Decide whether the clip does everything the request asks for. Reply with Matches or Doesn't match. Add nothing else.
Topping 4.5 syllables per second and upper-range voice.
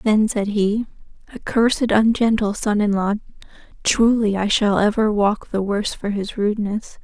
Matches